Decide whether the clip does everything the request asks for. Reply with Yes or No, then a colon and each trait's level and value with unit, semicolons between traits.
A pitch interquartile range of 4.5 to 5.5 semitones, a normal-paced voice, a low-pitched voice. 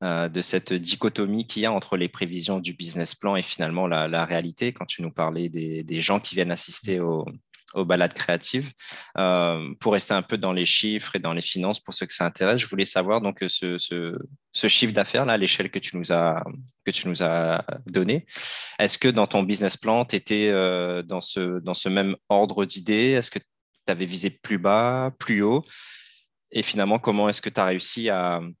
No: average, 3.3 semitones; average, 205 wpm; very low, 95 Hz